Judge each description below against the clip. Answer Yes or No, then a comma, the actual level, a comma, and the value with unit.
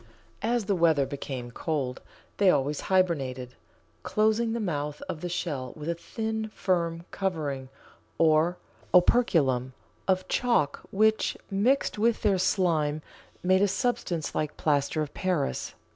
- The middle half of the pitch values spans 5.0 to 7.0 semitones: Yes, wide, 5.4 semitones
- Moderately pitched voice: Yes, medium, 170 Hz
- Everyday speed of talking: No, slow, 130 wpm